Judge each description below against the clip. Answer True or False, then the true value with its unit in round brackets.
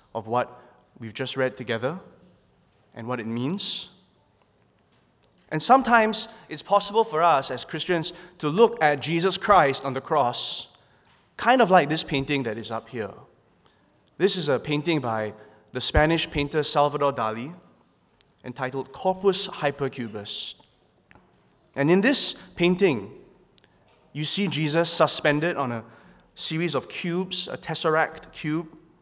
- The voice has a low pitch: False (150 Hz)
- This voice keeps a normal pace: False (130 wpm)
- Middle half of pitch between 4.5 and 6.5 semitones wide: True (5.6 semitones)